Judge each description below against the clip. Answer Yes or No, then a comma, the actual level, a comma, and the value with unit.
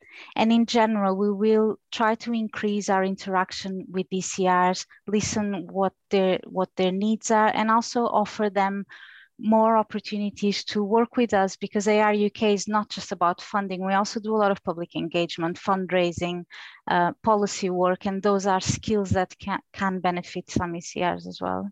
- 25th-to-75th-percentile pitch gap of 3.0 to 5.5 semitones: No, narrow, 2.6 semitones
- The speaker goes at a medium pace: Yes, average, 165 wpm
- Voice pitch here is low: No, high, 200 Hz